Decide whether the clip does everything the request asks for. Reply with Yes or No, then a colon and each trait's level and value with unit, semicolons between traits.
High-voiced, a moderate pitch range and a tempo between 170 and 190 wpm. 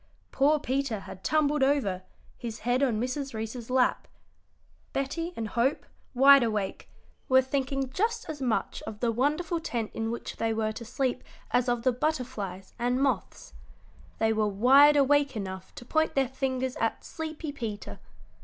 No: very high, 255 Hz; average, 3.8 semitones; average, 160 wpm